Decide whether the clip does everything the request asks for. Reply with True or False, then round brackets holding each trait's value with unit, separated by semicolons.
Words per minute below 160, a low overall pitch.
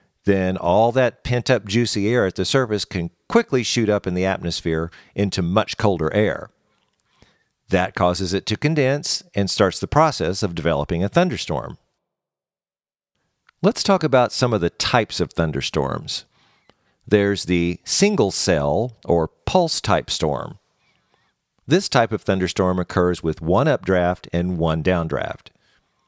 True (145 wpm; 100 Hz)